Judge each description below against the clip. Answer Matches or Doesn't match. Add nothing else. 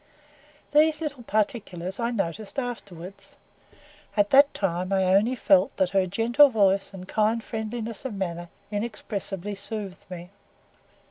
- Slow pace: Matches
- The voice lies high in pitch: Matches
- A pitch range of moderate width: Matches